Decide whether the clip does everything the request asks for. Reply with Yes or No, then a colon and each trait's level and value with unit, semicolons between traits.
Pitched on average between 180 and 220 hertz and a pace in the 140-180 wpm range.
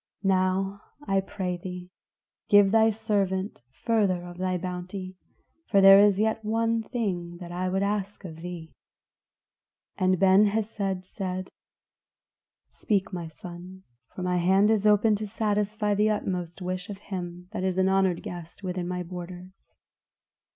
Yes: high, 190 Hz; average, 145 wpm